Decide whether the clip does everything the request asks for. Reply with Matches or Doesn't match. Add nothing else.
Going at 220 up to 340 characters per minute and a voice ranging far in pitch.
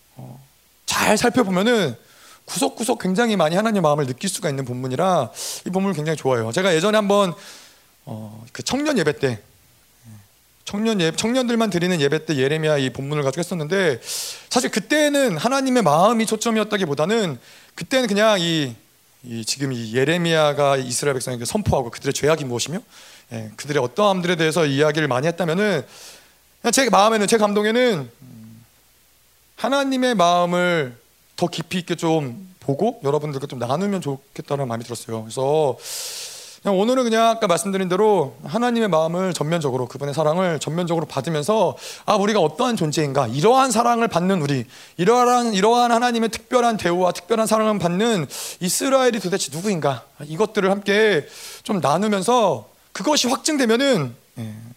Doesn't match